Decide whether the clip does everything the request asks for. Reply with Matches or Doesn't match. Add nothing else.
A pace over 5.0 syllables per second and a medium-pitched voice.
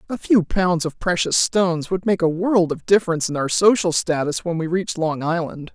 Matches